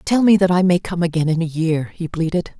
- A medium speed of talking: No, fast, 255 wpm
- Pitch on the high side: No, medium, 170 Hz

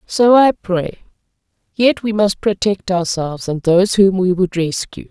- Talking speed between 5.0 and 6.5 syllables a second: No, 4.4 syllables/s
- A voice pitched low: No, high, 190 Hz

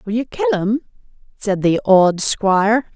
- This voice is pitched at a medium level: No, high, 215 Hz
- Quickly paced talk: No, average, 165 wpm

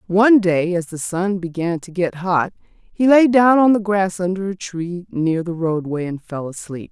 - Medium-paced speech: No, fast, 210 wpm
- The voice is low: No, medium, 185 Hz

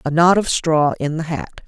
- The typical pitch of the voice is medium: Yes, medium, 160 Hz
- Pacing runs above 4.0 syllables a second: Yes, 4.7 syllables/s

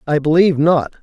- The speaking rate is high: No, average, 175 wpm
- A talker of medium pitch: Yes, medium, 155 Hz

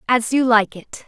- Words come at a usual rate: No, fast, 225 wpm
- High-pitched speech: Yes, high, 230 Hz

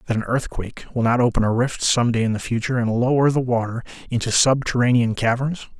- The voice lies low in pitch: Yes, low, 120 Hz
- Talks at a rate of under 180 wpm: No, average, 185 wpm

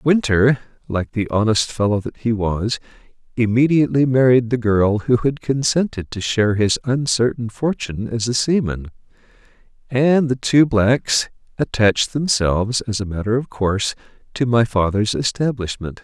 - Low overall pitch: Yes, low, 115 Hz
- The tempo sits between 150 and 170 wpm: No, average, 140 wpm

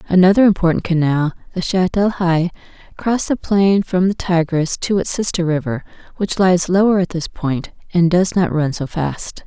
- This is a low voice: No, medium, 180 Hz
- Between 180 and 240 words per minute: Yes, average, 185 wpm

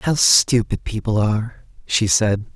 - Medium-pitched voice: No, low, 110 Hz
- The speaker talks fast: No, average, 140 wpm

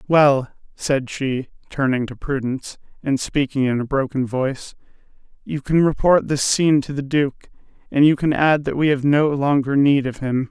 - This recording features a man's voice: Yes, male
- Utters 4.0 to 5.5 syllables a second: Yes, 4.8 syllables/s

